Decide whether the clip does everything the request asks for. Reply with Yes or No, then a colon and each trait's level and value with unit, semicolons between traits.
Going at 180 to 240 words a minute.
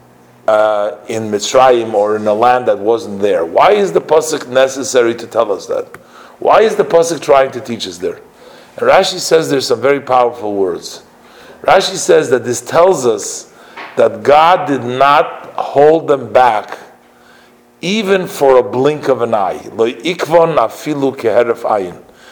No: average, 150 wpm